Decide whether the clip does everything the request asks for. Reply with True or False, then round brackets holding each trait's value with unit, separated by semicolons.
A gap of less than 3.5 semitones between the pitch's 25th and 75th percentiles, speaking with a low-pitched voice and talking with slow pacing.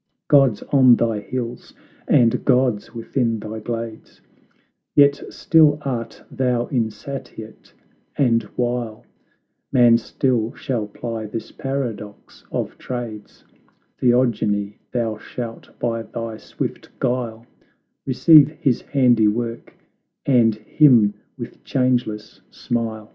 True (2.5 semitones; 120 Hz; 100 wpm)